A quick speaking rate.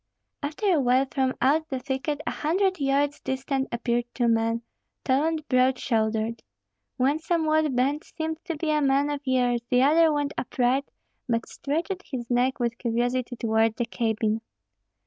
No: average, 165 wpm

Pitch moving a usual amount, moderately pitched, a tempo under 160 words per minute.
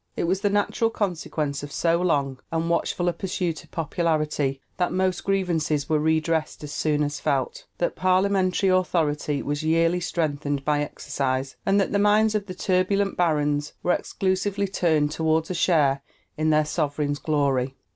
No: average, 3.9 semitones; medium, 165 Hz; average, 165 wpm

